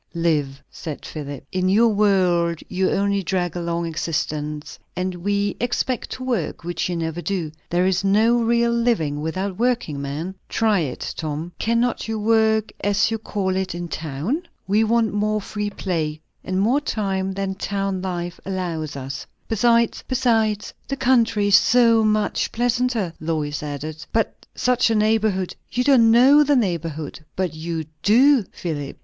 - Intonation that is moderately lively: Yes, average, 5.0 semitones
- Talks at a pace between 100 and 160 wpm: Yes, average, 155 wpm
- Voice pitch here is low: No, high, 195 Hz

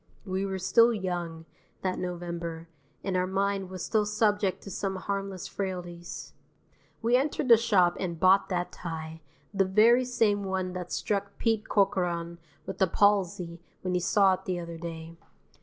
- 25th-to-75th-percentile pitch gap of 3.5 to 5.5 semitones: No, narrow, 2.6 semitones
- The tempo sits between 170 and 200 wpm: No, average, 160 wpm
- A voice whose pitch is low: No, medium, 185 Hz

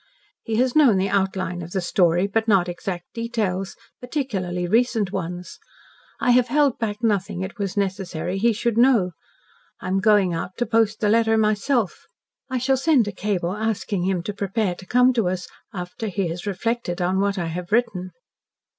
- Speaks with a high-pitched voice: Yes, high, 200 Hz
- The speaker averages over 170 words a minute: Yes, average, 180 wpm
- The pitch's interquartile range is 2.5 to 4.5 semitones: Yes, average, 3.9 semitones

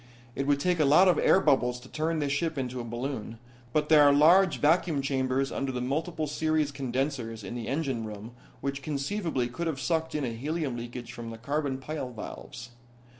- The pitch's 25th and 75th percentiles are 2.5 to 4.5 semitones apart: Yes, average, 3.9 semitones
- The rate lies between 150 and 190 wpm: No, average, 200 wpm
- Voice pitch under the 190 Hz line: Yes, medium, 140 Hz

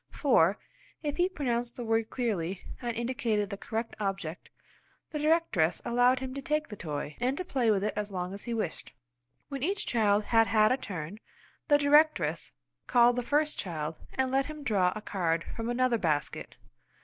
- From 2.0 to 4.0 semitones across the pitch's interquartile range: No, average, 5.1 semitones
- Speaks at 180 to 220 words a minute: Yes, average, 185 wpm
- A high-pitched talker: Yes, high, 230 Hz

